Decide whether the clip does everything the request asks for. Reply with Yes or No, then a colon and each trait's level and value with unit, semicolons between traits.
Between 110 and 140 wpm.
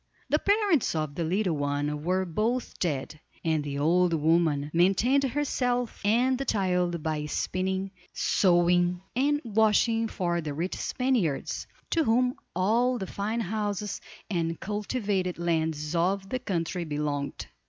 Yes: slow, 135 wpm